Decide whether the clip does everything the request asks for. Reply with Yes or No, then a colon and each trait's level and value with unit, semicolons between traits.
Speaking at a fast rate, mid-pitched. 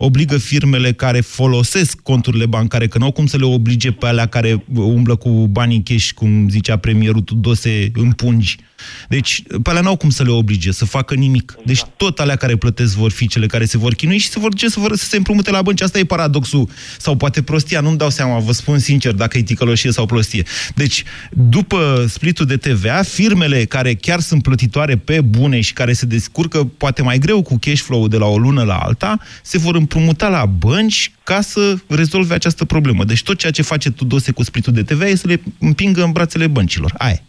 No: fast, 215 wpm; low, 130 Hz